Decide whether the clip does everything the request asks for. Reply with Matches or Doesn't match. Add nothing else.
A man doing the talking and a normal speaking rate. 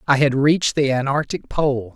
Matches